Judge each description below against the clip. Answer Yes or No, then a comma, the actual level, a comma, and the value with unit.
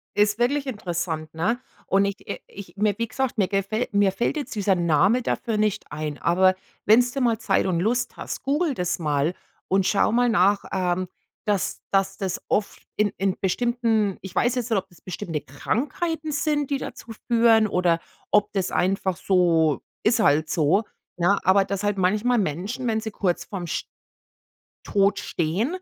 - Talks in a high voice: Yes, high, 200 Hz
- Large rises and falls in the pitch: No, average, 4.3 semitones